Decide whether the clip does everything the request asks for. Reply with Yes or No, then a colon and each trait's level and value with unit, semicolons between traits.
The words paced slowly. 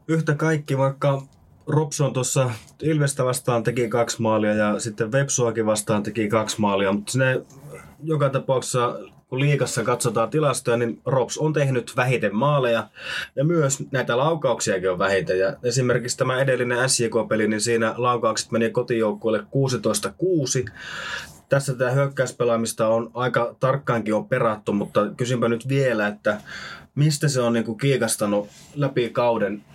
No: average, 135 wpm